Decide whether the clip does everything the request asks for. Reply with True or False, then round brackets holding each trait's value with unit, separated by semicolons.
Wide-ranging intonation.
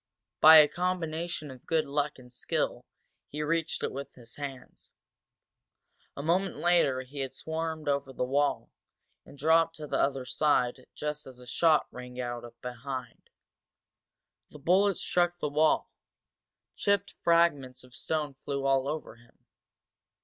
False (3.8 semitones)